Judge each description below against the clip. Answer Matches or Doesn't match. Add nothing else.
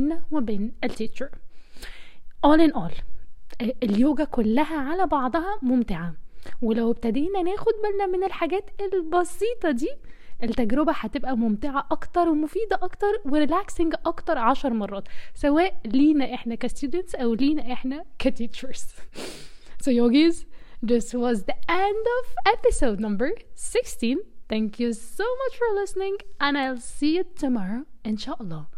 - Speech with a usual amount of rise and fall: Doesn't match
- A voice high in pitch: Matches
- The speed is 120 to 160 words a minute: Matches